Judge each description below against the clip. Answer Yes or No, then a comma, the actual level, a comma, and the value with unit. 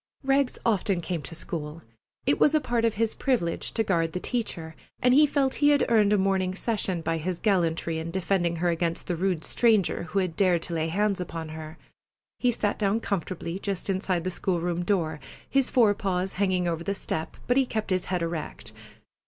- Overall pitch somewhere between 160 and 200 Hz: Yes, medium, 185 Hz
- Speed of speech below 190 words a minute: No, average, 200 wpm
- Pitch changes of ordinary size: Yes, average, 4.2 semitones